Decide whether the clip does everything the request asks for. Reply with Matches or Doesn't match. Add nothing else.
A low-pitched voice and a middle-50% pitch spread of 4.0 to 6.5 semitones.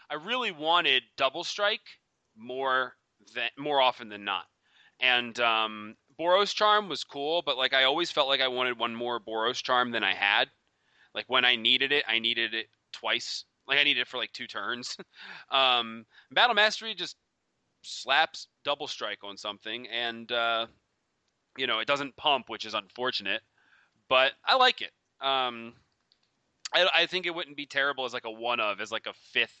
Matches